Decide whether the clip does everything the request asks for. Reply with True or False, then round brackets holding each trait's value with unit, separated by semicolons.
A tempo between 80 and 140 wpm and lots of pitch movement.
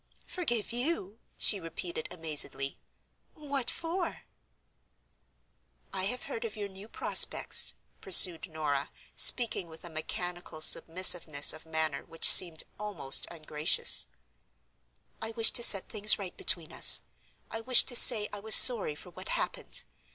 True (135 wpm; 5.9 semitones)